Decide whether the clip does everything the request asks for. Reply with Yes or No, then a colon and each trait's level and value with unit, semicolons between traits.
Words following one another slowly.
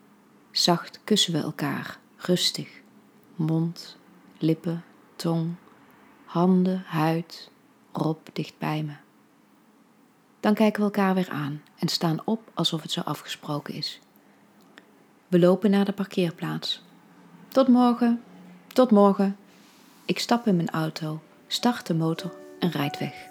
Yes: slow, 125 wpm